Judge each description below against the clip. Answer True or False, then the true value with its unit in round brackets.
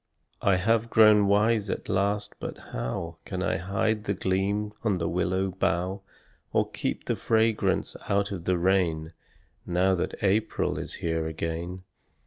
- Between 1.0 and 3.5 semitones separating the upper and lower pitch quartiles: True (2.8 semitones)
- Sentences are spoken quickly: False (150 wpm)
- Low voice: True (95 Hz)